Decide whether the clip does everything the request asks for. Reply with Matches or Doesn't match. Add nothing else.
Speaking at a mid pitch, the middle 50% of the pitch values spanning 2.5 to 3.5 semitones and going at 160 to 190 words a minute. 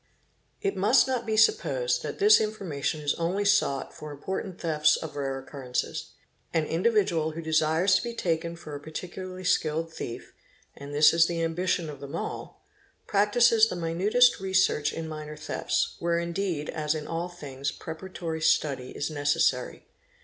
Doesn't match